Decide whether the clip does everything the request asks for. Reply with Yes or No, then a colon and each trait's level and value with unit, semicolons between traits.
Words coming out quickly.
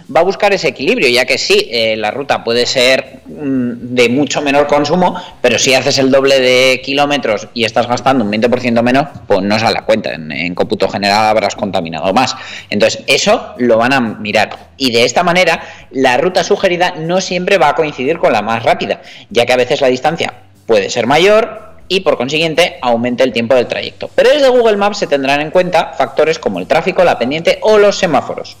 Yes: fast, 210 wpm